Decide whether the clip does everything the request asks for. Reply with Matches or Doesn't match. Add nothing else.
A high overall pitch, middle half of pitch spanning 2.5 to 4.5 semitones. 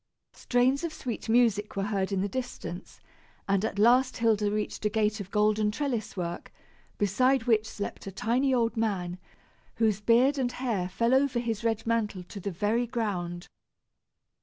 Matches